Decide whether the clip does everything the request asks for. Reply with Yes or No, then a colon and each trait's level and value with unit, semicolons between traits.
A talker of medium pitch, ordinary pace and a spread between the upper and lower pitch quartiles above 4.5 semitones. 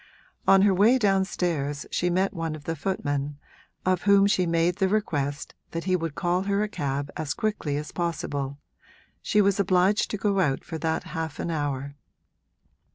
Yes: medium, 175 Hz; average, 170 wpm; average, 4.9 semitones